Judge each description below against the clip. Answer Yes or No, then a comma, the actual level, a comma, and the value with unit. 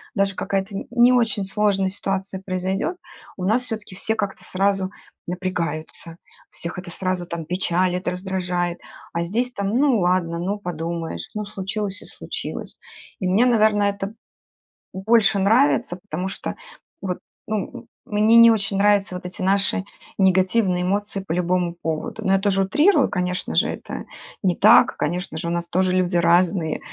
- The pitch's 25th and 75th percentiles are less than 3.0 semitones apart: Yes, narrow, 2.5 semitones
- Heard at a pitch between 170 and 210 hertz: Yes, high, 190 Hz